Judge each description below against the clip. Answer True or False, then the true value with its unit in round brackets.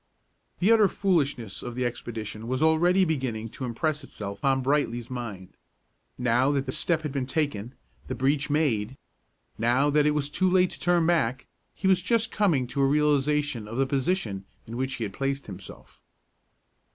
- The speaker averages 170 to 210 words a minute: True (175 wpm)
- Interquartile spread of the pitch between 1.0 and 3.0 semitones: False (4.6 semitones)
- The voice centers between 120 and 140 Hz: True (135 Hz)